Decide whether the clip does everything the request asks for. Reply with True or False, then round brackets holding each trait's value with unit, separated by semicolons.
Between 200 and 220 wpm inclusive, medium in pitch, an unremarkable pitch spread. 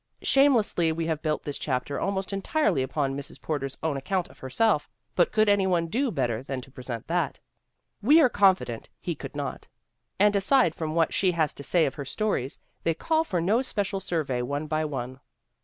False (205 wpm; 165 Hz; 6.4 semitones)